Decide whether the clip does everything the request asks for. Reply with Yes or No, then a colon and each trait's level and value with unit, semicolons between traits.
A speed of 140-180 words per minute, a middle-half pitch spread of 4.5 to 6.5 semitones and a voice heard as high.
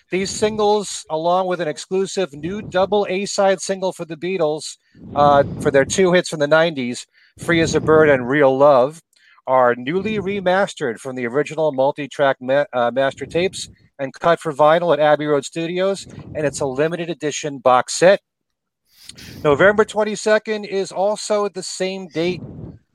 No: average, 165 wpm; average, 5.0 semitones; medium, 160 Hz